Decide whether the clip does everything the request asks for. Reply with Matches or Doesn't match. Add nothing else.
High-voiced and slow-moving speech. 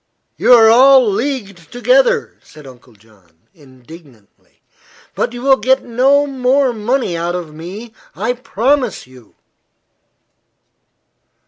Matches